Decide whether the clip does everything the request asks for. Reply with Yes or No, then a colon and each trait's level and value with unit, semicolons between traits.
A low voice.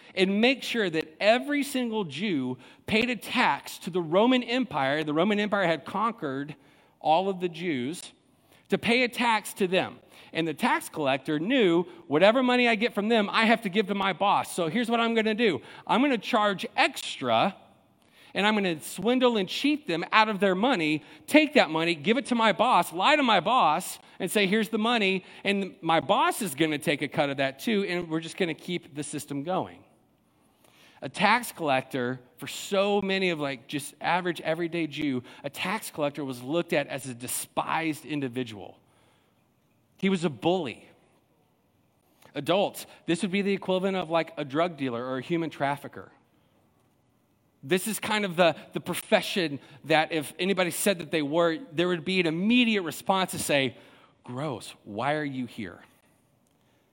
No: medium, 180 Hz